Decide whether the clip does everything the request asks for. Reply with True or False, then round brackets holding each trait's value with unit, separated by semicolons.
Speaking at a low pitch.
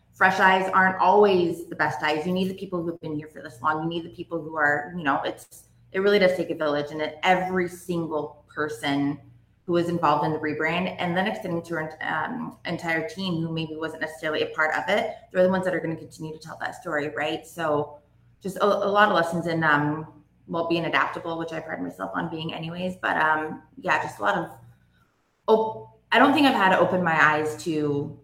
False (160 Hz)